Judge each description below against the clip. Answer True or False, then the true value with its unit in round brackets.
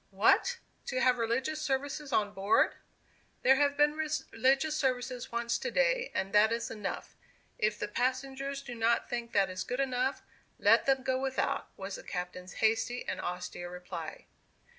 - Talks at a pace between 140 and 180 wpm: True (160 wpm)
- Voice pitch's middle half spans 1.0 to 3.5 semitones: False (4.3 semitones)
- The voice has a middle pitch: False (250 Hz)